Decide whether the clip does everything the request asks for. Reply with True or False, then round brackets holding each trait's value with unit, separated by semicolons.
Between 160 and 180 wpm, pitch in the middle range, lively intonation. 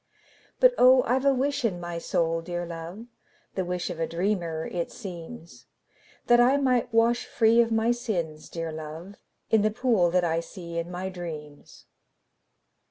True (170 wpm; 180 Hz; 5.8 semitones)